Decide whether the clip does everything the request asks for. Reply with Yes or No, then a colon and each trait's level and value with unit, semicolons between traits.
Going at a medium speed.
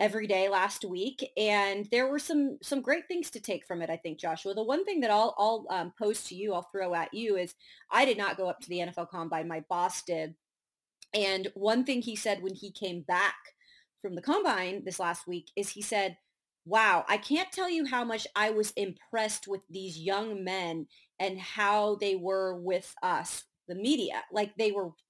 No: fast, 210 wpm